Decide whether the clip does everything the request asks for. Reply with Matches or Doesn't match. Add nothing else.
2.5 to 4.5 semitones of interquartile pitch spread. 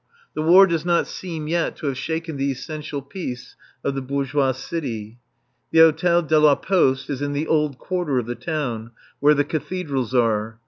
Matches